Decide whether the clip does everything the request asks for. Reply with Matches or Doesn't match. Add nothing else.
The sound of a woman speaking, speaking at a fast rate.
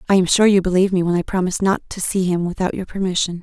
Matches